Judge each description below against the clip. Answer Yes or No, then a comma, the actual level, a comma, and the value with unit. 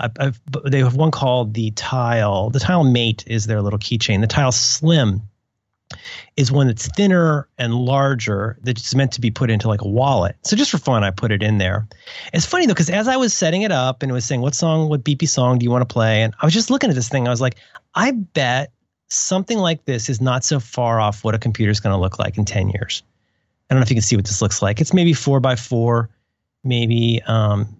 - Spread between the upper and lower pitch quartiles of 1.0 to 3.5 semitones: No, average, 4.2 semitones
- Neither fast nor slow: No, fast, 250 wpm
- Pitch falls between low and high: No, low, 125 Hz